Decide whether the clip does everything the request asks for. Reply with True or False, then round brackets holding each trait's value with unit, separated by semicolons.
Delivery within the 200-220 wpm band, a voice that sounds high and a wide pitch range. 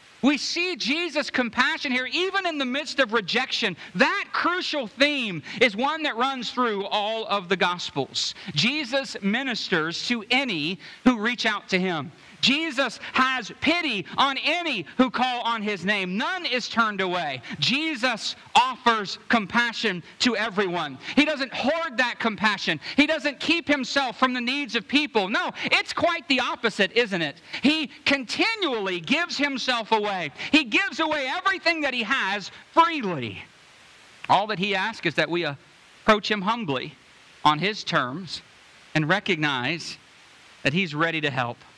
False (150 wpm; 240 Hz; 6.2 semitones)